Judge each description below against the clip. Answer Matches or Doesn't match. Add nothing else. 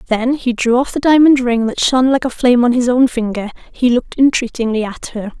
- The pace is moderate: Doesn't match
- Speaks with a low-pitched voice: Doesn't match